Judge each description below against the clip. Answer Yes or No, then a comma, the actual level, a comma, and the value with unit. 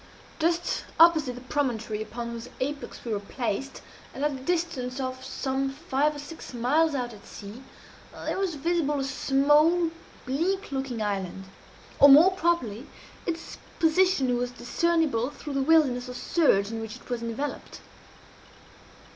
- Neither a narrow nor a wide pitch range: Yes, average, 4.9 semitones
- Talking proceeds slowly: No, average, 150 wpm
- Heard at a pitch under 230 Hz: No, very high, 270 Hz